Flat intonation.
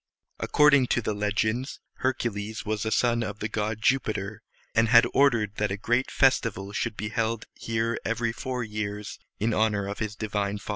Yes: narrow, 2.2 semitones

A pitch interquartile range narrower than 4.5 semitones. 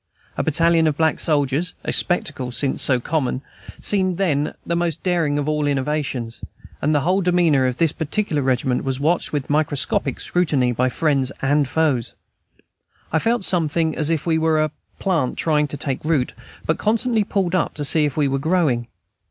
Yes: average, 3.4 semitones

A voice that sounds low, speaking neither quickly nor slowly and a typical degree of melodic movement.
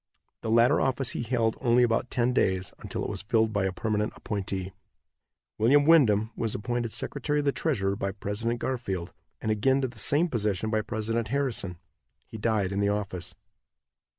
Yes: low, 110 Hz; average, 180 wpm; average, 3.2 semitones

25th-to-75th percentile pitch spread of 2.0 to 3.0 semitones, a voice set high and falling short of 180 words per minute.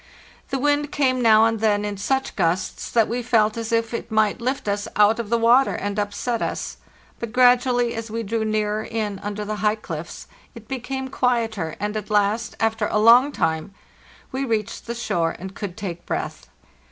No: narrow, 2.5 semitones; high, 220 Hz; average, 190 wpm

